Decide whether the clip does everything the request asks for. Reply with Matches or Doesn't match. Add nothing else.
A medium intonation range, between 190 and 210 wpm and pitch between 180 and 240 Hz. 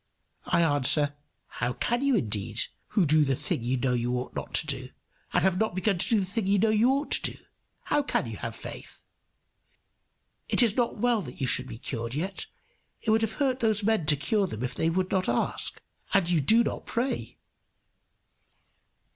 Doesn't match